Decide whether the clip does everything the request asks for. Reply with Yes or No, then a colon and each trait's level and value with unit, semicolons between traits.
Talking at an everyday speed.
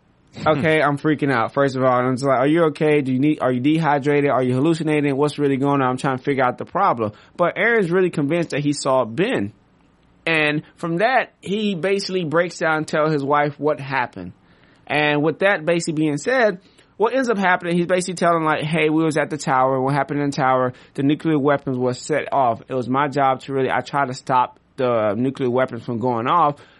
No: fast, 225 wpm